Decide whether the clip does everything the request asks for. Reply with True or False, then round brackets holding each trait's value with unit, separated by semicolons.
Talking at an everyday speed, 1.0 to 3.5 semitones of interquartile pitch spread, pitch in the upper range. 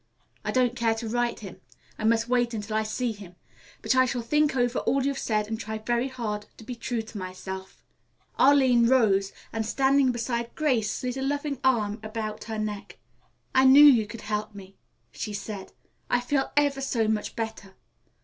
True (190 wpm; 3.2 semitones; 230 Hz)